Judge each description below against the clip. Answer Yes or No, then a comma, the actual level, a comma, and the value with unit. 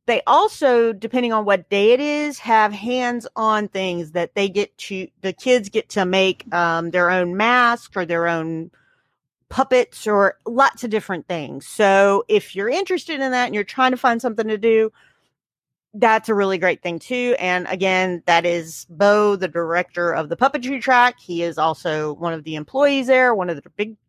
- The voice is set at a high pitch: Yes, high, 205 Hz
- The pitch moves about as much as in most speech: No, wide, 5.8 semitones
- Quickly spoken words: No, average, 190 wpm